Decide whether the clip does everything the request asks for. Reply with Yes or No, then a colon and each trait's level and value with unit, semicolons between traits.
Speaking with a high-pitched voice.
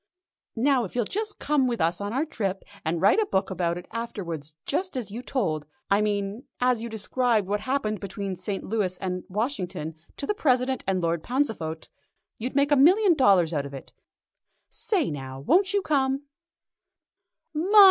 Yes: high, 215 Hz